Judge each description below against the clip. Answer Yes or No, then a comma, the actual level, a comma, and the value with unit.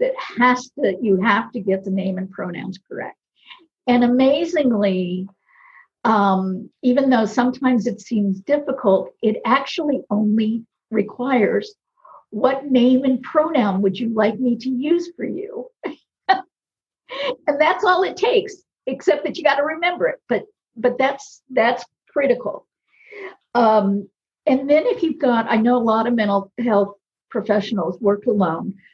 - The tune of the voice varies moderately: No, wide, 6.6 semitones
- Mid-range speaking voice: No, very high, 250 Hz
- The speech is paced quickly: No, average, 145 wpm